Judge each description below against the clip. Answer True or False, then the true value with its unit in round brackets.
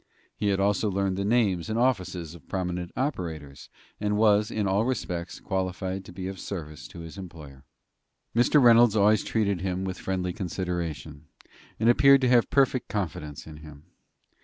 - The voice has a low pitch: True (95 Hz)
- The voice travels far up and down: False (3.8 semitones)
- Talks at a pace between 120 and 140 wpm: False (165 wpm)